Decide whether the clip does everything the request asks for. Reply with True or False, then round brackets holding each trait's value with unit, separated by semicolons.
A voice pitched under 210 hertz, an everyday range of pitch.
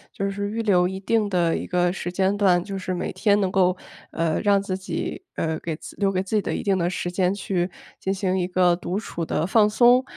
False (190 Hz; 2.2 semitones)